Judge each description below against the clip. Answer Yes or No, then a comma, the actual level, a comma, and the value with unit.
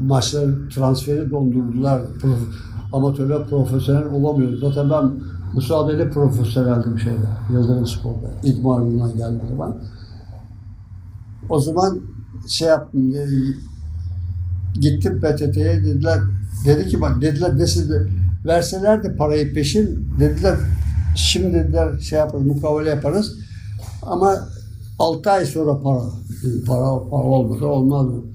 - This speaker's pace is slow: No, average, 110 wpm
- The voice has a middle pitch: No, low, 125 Hz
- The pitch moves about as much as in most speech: No, wide, 5.8 semitones